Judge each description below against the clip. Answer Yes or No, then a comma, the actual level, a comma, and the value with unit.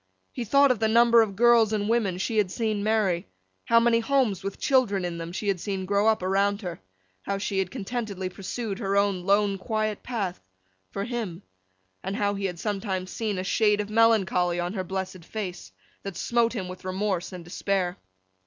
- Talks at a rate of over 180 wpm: Yes, average, 190 wpm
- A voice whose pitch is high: Yes, high, 200 Hz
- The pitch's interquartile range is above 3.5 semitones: No, average, 3.1 semitones